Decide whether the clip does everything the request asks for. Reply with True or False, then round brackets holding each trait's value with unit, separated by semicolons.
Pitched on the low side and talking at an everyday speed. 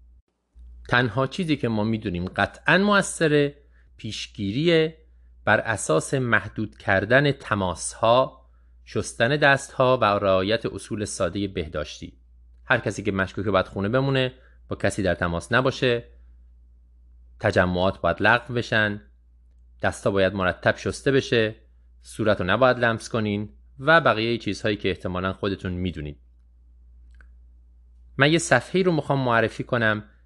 True (100 Hz; 125 wpm)